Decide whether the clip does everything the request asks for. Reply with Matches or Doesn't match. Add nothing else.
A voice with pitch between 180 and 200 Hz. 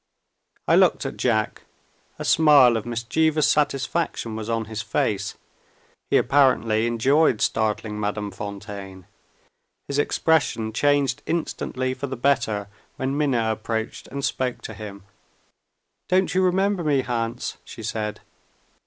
Doesn't match